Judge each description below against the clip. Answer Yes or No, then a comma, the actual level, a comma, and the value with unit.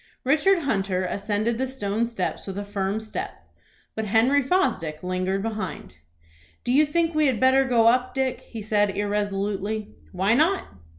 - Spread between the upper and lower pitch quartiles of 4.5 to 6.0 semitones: Yes, average, 4.9 semitones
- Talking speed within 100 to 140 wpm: No, average, 160 wpm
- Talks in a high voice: Yes, high, 220 Hz